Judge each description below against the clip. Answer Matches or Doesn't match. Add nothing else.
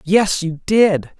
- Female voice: Doesn't match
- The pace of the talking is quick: Doesn't match